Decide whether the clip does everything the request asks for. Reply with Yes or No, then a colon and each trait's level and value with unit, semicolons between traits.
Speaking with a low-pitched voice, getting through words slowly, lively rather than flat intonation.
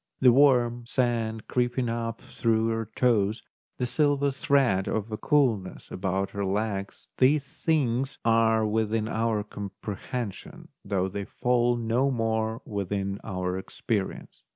No: low, 115 Hz; slow, 125 wpm; average, 3.4 semitones